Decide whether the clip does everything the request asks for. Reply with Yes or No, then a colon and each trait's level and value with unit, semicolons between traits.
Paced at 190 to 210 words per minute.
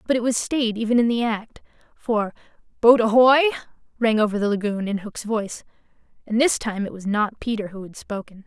Yes: average, 200 wpm